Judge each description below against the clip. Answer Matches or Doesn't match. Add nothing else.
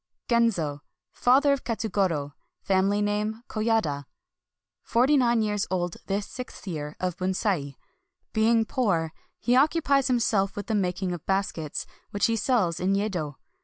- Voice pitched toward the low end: Doesn't match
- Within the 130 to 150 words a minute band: Matches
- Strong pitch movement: Doesn't match